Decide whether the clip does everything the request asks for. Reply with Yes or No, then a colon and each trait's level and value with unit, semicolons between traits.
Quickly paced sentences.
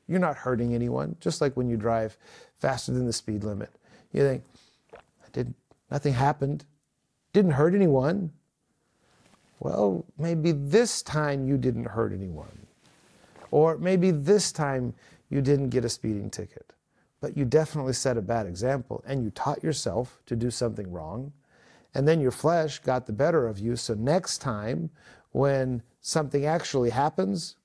No: average, 155 wpm